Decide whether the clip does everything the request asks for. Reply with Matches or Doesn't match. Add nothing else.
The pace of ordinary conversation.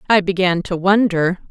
Matches